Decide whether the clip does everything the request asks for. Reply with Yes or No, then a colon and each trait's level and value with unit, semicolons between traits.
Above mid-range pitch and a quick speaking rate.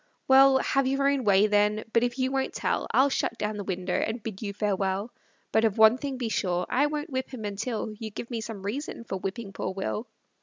Yes: high, 220 Hz; fast, 230 wpm